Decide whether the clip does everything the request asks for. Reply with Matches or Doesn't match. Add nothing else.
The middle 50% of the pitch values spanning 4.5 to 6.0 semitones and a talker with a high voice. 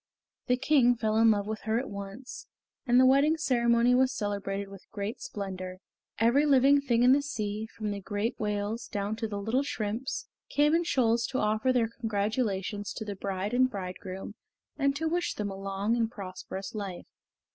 Doesn't match